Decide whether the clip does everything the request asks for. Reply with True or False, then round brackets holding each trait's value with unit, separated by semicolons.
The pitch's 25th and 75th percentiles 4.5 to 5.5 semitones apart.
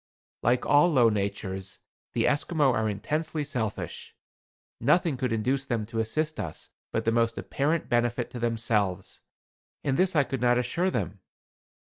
True (4.8 semitones)